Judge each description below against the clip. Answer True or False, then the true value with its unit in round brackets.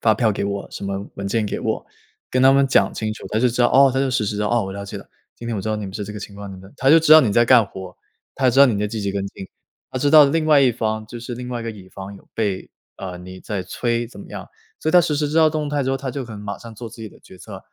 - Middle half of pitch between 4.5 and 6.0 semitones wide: True (4.8 semitones)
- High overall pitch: False (115 Hz)